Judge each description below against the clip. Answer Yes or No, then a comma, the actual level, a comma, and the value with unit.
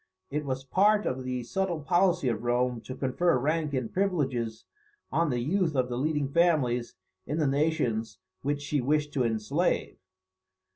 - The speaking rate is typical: Yes, average, 160 wpm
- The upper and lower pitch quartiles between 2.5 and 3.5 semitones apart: No, average, 4.4 semitones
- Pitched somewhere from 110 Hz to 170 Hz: Yes, medium, 140 Hz